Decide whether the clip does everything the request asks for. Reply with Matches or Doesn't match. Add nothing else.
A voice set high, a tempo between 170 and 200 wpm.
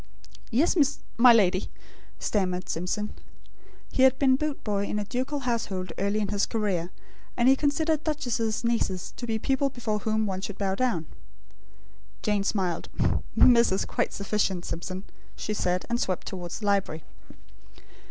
Doesn't match